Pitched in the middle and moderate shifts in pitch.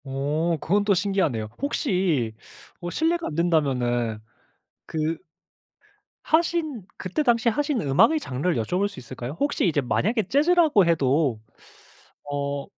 No: medium, 170 Hz; wide, 8.9 semitones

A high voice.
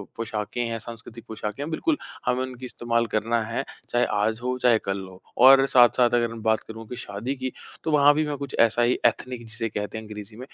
No: low, 115 Hz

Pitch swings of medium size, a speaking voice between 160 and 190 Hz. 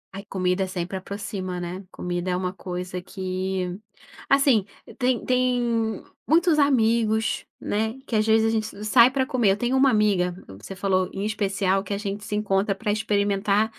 No: average, 3.1 semitones; high, 205 Hz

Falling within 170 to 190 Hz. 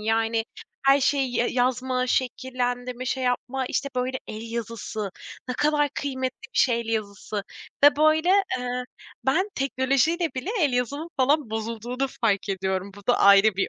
No: very high, 250 Hz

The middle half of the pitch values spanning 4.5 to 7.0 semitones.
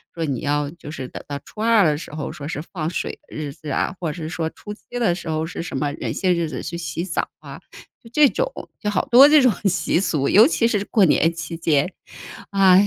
Yes: average, 5.0 semitones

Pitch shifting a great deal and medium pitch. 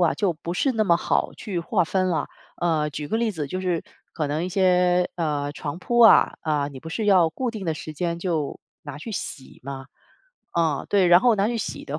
No: average, 4.1 semitones; medium, 175 Hz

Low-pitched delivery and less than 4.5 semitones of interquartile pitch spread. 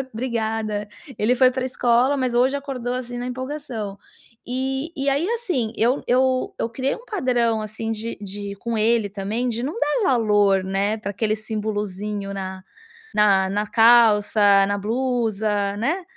No: high, 225 Hz; average, 3.6 semitones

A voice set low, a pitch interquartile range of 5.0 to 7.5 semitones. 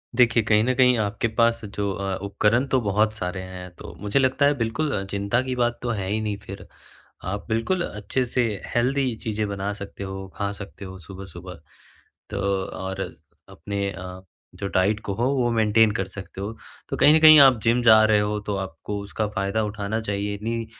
No: low, 105 Hz; average, 2.9 semitones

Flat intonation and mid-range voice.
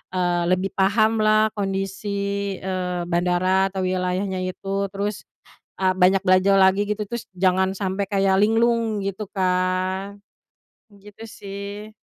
No: narrow, 1.6 semitones; high, 195 Hz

